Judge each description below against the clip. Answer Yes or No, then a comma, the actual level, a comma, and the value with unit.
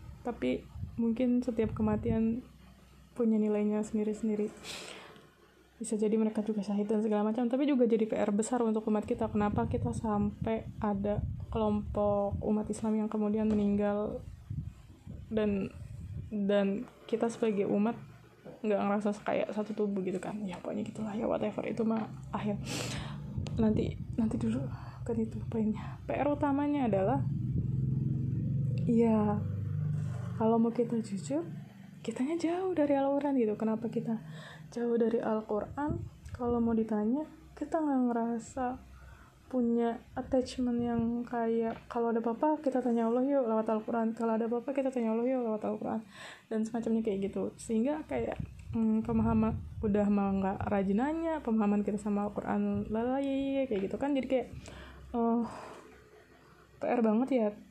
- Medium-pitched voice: No, high, 220 Hz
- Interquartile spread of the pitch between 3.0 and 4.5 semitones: No, narrow, 2.6 semitones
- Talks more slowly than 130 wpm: No, fast, 140 wpm